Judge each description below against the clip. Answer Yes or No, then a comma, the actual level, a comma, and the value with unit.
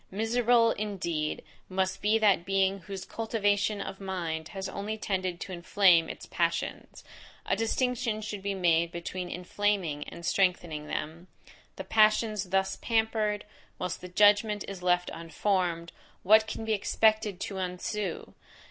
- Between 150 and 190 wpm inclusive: No, average, 140 wpm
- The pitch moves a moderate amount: Yes, average, 3.1 semitones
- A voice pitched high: Yes, high, 195 Hz